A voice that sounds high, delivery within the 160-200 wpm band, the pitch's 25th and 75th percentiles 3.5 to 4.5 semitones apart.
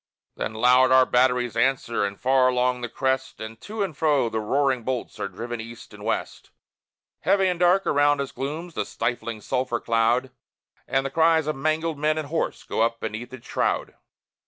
No: low, 130 Hz; average, 185 wpm; average, 4.1 semitones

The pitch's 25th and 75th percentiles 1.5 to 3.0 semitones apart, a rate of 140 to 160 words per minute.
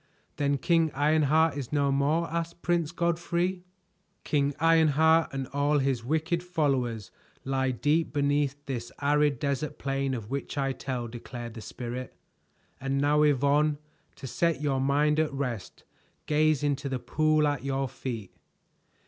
Yes: narrow, 2.5 semitones; average, 145 wpm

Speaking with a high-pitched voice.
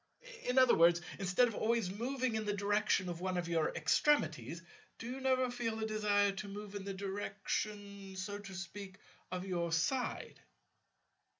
Yes: high, 200 Hz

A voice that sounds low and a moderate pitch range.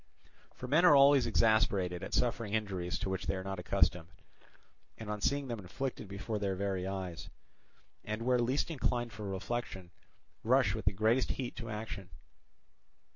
Yes: low, 105 Hz; average, 4.1 semitones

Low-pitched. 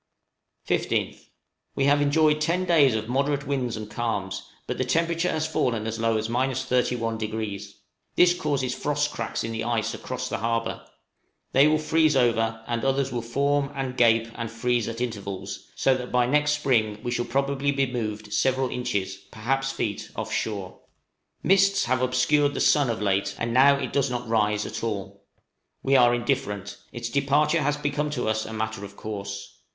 Yes: low, 125 Hz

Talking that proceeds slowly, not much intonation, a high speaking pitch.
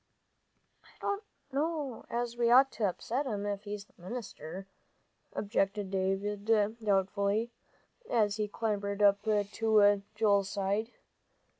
Yes: slow, 120 wpm; narrow, 2.3 semitones; high, 205 Hz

